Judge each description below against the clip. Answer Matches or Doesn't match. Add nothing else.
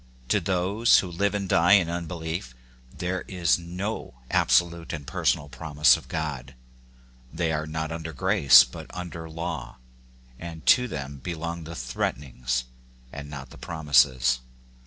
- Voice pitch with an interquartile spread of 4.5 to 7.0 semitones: Doesn't match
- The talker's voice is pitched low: Matches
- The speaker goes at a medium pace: Matches